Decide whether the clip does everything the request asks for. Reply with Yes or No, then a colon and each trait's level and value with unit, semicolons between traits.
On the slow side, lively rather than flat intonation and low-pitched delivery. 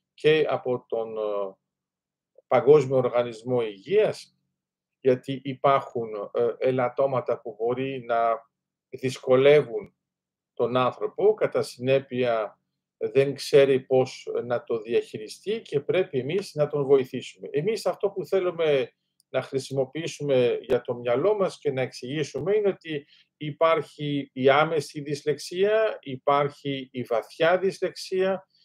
No: slow, 110 wpm; wide, 6.8 semitones; medium, 145 Hz